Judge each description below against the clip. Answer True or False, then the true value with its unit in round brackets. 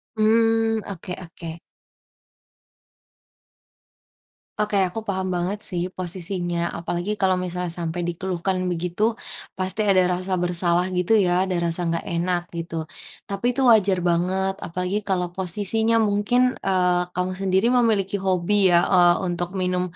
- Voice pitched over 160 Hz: True (185 Hz)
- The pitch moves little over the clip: True (2.1 semitones)